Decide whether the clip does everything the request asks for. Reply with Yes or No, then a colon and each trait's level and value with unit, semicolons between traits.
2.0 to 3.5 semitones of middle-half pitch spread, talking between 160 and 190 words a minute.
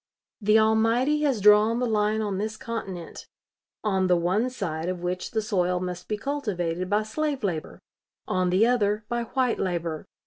No: average, 3.9 semitones; average, 170 wpm